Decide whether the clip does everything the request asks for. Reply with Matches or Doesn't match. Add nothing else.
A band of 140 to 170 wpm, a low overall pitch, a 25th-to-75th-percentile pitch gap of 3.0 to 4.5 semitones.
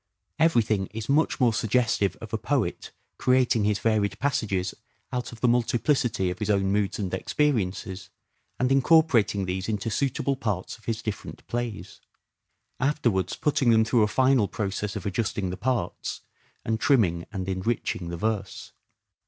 Matches